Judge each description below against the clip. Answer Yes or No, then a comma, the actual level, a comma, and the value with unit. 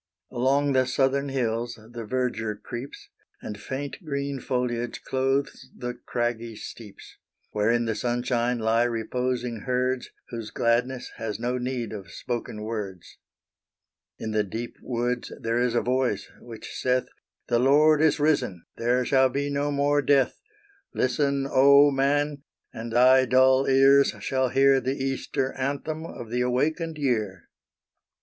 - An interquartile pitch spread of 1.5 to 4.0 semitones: Yes, narrow, 2.6 semitones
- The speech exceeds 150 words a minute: No, average, 140 wpm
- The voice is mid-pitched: No, low, 125 Hz